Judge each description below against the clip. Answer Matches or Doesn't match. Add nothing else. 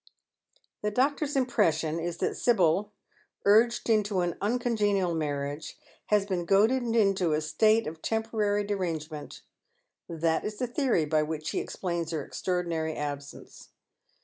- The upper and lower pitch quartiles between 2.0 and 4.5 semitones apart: Doesn't match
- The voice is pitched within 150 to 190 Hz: Matches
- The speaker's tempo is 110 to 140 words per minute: Matches